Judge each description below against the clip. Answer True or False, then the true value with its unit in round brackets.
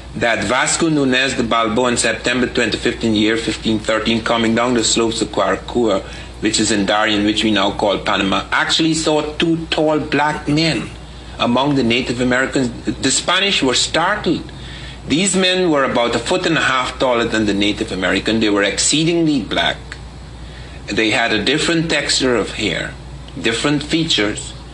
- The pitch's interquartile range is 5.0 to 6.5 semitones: True (5.6 semitones)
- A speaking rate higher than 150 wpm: True (165 wpm)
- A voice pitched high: False (115 Hz)